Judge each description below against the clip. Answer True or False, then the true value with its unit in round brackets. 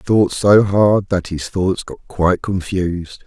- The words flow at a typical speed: True (185 wpm)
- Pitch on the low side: True (95 Hz)